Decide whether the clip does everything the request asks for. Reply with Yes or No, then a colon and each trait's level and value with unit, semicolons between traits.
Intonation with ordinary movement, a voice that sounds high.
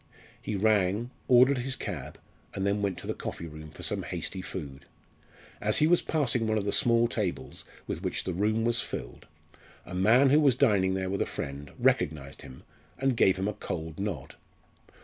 No: average, 4.7 semitones; low, 100 Hz